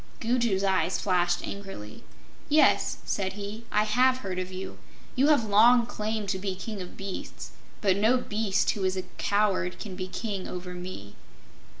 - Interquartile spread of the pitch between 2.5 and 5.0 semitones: Yes, average, 2.9 semitones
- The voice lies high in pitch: Yes, high, 200 Hz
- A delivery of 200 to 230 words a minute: No, average, 170 wpm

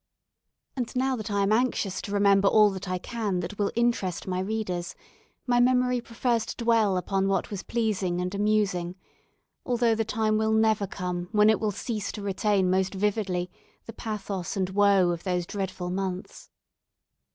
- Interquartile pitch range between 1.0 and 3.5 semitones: Yes, average, 3.0 semitones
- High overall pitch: Yes, high, 205 Hz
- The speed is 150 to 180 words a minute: Yes, average, 170 wpm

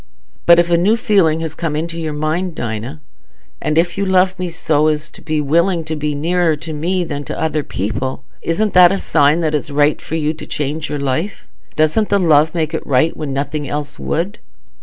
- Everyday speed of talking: No, fast, 215 wpm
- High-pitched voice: No, medium, 155 Hz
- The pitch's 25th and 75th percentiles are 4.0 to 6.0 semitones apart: No, narrow, 2.6 semitones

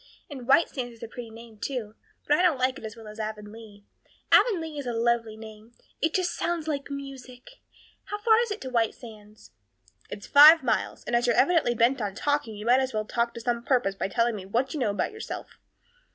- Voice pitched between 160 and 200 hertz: No, high, 240 Hz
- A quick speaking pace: Yes, fast, 225 wpm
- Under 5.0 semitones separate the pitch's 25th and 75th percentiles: Yes, average, 4.4 semitones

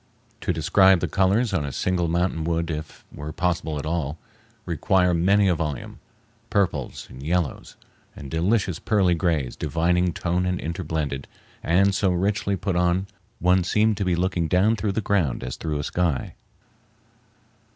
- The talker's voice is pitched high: No, very low, 90 Hz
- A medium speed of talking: Yes, average, 160 wpm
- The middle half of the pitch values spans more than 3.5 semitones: No, average, 3.1 semitones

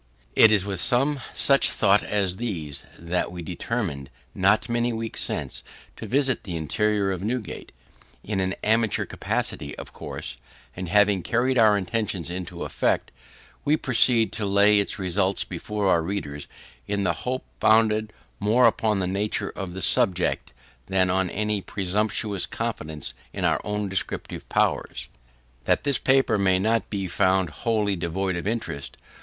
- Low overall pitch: Yes, low, 100 Hz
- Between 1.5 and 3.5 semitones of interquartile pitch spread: Yes, average, 3.2 semitones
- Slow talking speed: No, average, 155 wpm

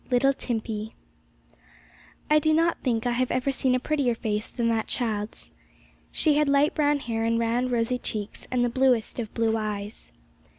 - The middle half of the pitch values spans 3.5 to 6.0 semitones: No, average, 3.1 semitones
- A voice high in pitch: Yes, high, 245 Hz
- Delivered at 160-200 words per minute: Yes, average, 175 wpm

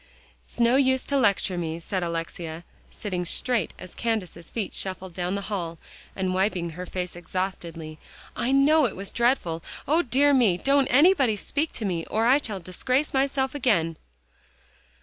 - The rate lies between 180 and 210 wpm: No, average, 165 wpm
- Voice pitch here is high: Yes, high, 200 Hz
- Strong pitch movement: Yes, wide, 7.0 semitones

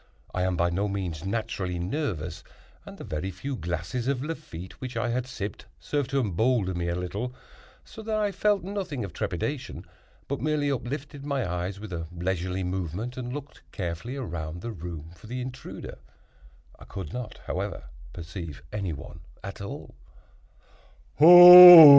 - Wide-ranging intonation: Yes, wide, 6.8 semitones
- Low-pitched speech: Yes, low, 100 Hz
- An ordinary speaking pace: Yes, average, 160 wpm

